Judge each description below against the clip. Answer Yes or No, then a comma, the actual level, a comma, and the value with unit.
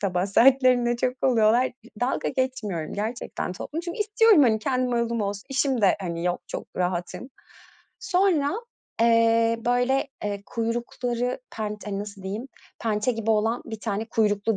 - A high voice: Yes, high, 230 Hz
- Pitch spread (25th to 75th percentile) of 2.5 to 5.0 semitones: Yes, average, 3.5 semitones